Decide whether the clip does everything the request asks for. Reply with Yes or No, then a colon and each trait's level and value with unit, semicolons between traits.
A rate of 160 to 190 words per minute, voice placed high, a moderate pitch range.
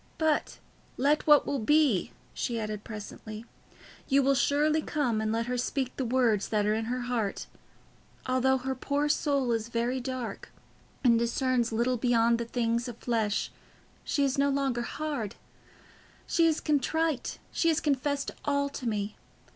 Yes: average, 165 wpm; very high, 250 Hz; average, 3.6 semitones